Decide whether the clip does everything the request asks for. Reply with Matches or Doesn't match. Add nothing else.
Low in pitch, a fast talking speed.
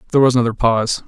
Matches